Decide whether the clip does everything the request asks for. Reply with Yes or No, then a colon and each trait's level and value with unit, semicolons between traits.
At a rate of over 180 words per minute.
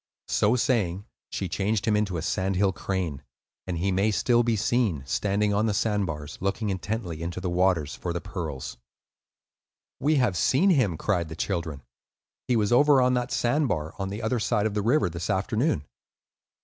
Yes: average, 190 wpm